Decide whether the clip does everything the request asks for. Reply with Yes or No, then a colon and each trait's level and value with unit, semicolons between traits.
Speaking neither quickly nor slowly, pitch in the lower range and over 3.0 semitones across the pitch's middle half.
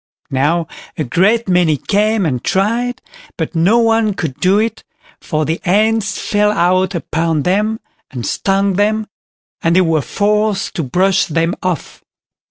No: average, 150 wpm; high, 190 Hz; average, 4.3 semitones